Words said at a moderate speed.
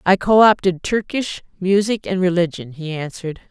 Yes: average, 155 wpm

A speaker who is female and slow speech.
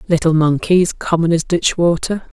Yes: female; slow, 125 wpm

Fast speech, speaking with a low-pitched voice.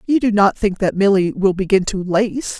No: fast, 230 wpm; high, 200 Hz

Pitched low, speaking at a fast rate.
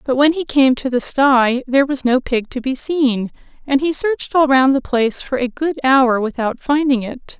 No: very high, 265 Hz; fast, 225 wpm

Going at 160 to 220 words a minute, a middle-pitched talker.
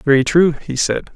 Yes: fast, 205 wpm; medium, 150 Hz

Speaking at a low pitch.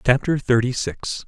Yes: low, 125 Hz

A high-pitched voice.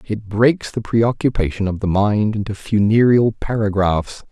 No: low, 105 Hz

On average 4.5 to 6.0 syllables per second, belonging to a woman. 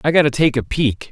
No: 5.9 syllables/s; male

